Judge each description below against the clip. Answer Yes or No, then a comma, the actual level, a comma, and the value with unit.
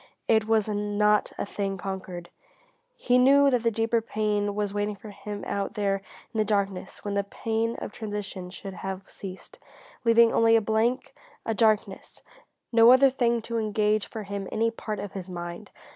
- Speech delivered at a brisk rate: No, average, 175 wpm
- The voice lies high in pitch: Yes, high, 210 Hz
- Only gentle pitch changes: Yes, narrow, 2.2 semitones